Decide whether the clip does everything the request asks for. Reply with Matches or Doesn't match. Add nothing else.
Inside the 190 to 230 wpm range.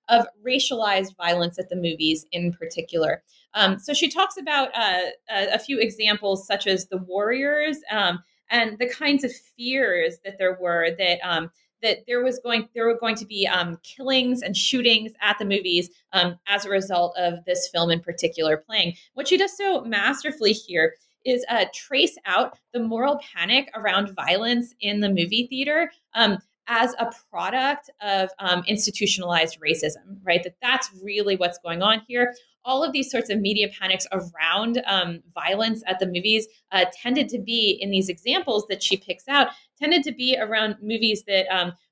Doesn't match